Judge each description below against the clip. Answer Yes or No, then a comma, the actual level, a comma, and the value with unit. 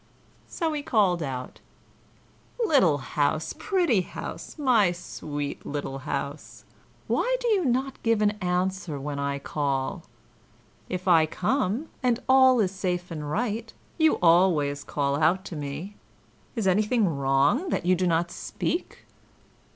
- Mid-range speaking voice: Yes, medium, 180 Hz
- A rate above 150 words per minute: No, slow, 135 wpm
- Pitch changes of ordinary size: No, wide, 8.1 semitones